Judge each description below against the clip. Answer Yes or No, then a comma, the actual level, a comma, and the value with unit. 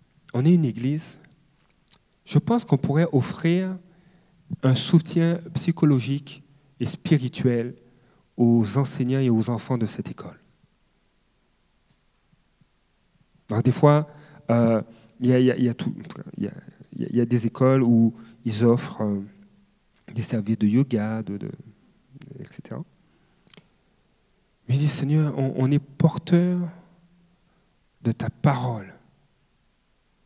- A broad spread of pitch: Yes, wide, 5.8 semitones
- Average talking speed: No, slow, 120 wpm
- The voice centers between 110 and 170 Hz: Yes, medium, 140 Hz